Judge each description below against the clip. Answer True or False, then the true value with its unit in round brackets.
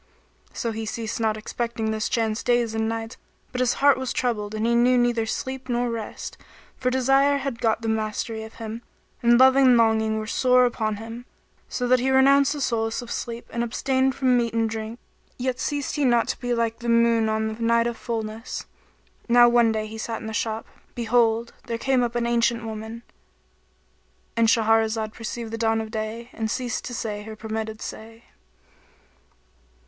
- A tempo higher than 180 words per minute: True (190 wpm)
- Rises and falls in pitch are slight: True (1.7 semitones)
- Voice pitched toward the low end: False (230 Hz)